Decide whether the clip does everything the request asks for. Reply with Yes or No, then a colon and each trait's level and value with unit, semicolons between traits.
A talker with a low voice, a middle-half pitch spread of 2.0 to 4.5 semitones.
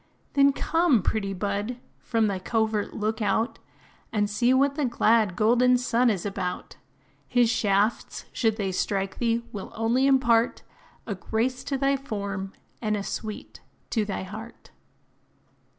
No: high, 220 Hz; average, 3.4 semitones